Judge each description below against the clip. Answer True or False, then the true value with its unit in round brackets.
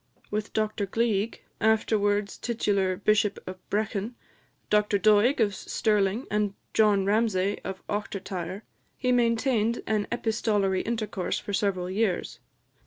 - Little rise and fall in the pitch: True (1.9 semitones)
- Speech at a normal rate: False (115 wpm)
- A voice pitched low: False (210 Hz)